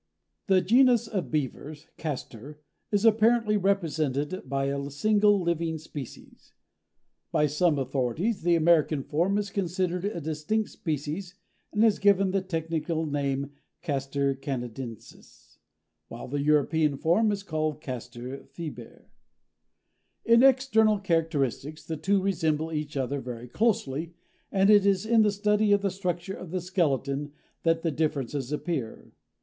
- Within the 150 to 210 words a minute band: No, slow, 135 wpm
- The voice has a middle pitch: Yes, medium, 160 Hz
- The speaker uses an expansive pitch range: Yes, wide, 5.7 semitones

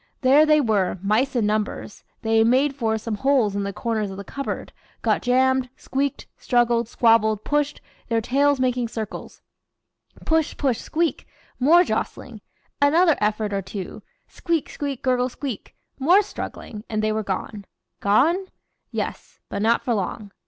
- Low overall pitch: No, high, 240 Hz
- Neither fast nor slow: Yes, average, 150 wpm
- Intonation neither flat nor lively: Yes, average, 4.7 semitones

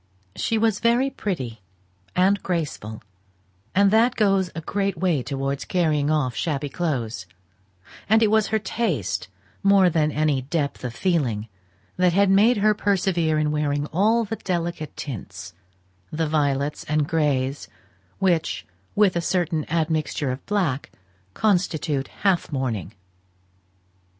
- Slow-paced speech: Yes, slow, 130 wpm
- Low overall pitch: No, medium, 160 Hz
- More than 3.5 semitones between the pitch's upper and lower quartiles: Yes, wide, 5.6 semitones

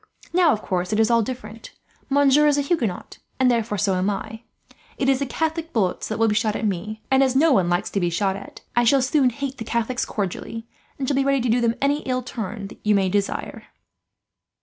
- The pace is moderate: No, fast, 235 wpm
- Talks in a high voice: Yes, high, 230 Hz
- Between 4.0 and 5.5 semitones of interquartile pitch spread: Yes, average, 4.6 semitones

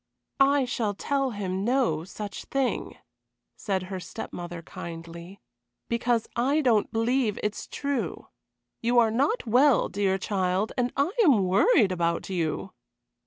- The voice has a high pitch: Yes, high, 215 Hz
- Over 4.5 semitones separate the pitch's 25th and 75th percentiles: Yes, average, 5.3 semitones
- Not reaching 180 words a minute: Yes, average, 140 wpm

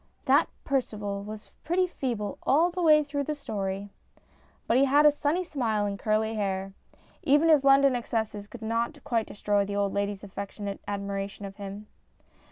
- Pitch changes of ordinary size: No, wide, 5.7 semitones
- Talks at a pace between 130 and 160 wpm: No, average, 170 wpm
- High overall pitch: Yes, high, 220 Hz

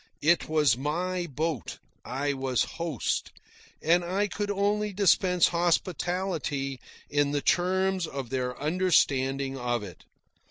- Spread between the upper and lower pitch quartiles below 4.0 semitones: No, average, 5.2 semitones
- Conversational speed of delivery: No, slow, 120 wpm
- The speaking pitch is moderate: Yes, medium, 160 Hz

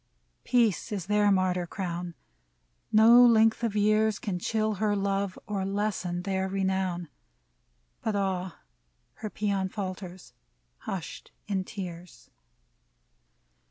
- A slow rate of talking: Yes, slow, 115 wpm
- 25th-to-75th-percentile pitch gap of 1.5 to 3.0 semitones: Yes, narrow, 2.6 semitones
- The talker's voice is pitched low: No, high, 195 Hz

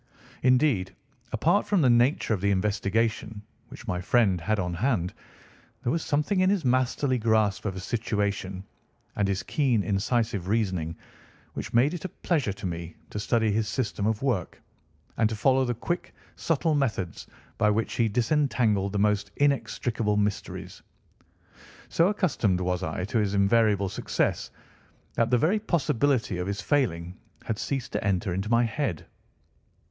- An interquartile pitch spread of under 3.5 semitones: No, average, 4.8 semitones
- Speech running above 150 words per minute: Yes, average, 160 wpm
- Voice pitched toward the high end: No, low, 110 Hz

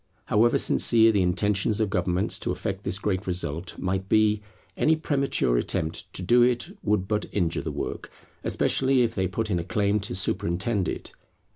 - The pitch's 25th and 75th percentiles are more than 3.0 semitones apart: Yes, average, 3.4 semitones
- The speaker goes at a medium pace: Yes, average, 175 wpm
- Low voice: Yes, low, 100 Hz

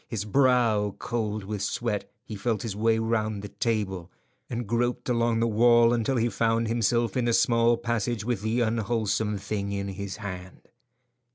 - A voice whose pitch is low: Yes, low, 115 Hz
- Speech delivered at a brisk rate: No, average, 170 wpm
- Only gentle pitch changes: Yes, narrow, 2.3 semitones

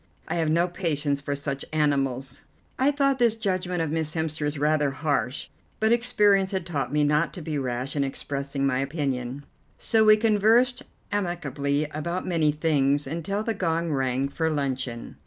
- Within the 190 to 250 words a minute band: No, average, 165 wpm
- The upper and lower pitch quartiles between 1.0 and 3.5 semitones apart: No, average, 4.8 semitones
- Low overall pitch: No, medium, 155 Hz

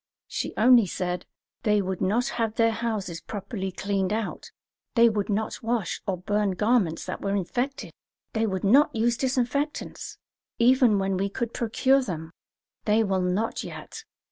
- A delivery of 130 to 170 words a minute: Yes, average, 155 wpm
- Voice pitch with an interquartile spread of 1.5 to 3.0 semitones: No, average, 3.5 semitones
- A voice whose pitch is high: Yes, high, 215 Hz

